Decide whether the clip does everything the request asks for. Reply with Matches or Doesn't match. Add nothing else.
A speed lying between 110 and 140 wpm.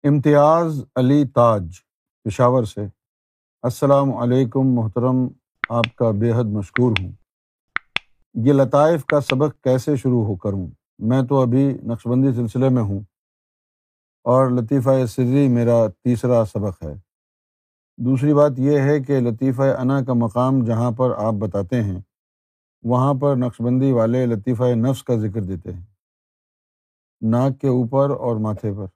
Matches